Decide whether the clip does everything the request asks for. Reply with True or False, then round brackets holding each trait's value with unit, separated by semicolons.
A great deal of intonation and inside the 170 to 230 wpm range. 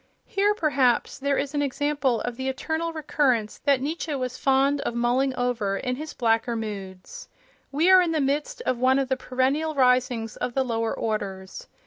False (3.4 semitones; 180 wpm)